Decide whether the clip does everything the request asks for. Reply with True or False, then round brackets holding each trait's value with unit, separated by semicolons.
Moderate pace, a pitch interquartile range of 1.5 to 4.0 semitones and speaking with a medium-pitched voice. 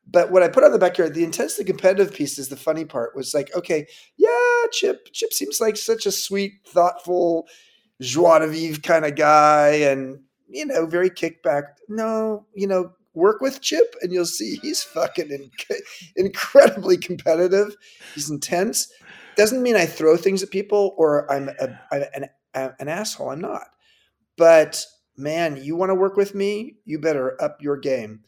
False (180 wpm; 5.3 semitones; 180 Hz)